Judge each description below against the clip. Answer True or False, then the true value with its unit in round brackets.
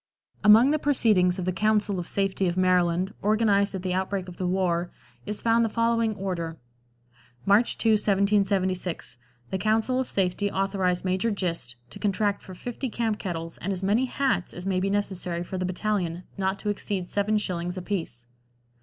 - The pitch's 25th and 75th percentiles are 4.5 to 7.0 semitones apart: False (2.7 semitones)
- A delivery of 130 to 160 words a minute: False (175 wpm)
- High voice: True (195 Hz)